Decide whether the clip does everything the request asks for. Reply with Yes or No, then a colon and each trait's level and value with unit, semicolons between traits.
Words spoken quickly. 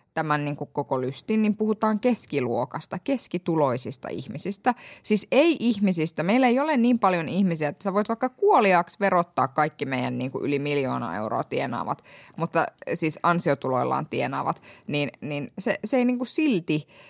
Yes: fast, 160 wpm